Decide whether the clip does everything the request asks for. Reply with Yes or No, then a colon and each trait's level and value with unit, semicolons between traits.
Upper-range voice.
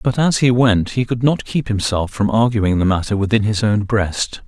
No: low, 110 Hz